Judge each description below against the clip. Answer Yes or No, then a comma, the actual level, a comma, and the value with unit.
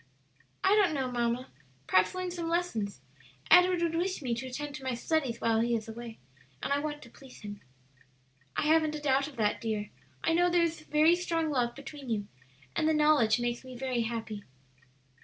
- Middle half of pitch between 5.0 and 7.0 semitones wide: Yes, wide, 5.4 semitones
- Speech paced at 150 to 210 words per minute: Yes, average, 195 wpm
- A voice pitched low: No, very high, 270 Hz